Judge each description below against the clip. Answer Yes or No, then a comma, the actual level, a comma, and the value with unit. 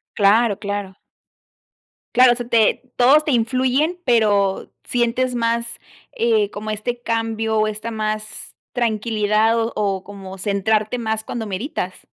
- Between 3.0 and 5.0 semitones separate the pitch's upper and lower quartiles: No, narrow, 2.4 semitones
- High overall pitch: Yes, high, 225 Hz